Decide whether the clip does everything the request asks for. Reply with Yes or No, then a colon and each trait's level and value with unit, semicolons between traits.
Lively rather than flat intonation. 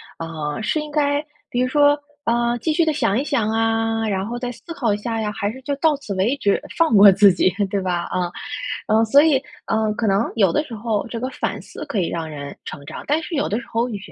Yes: wide, 5.7 semitones